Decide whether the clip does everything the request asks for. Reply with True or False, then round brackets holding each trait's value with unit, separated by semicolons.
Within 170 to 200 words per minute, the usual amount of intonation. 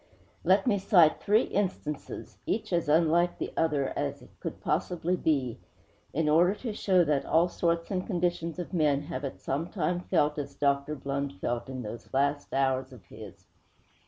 True (175 wpm; 4.1 semitones)